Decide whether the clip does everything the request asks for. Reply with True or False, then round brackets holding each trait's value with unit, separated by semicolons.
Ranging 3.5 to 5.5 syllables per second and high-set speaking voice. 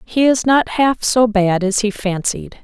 True (4.0 syllables/s; 225 Hz)